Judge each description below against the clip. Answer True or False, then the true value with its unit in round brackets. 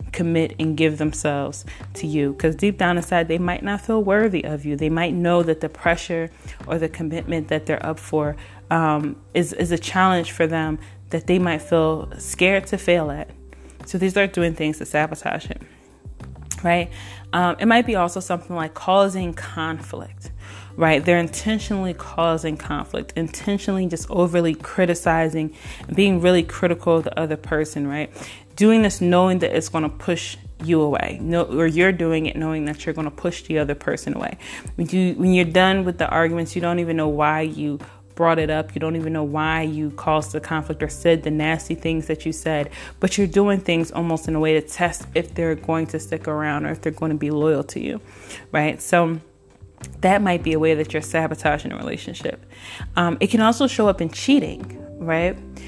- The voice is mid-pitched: True (160 Hz)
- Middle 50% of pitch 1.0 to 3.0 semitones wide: True (2.4 semitones)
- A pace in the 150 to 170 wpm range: False (200 wpm)